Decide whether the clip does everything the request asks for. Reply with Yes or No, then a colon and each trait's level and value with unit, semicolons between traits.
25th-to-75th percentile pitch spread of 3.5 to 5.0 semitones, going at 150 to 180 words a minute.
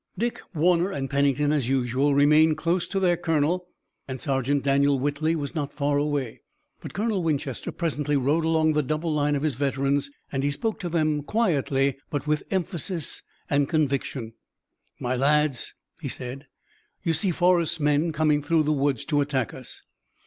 No: average, 2.7 semitones; average, 170 wpm